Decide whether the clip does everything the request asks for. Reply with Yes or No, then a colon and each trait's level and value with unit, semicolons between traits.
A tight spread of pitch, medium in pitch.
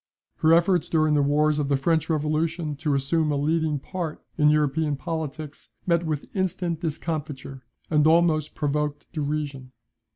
Yes: narrow, 1.9 semitones; medium, 155 Hz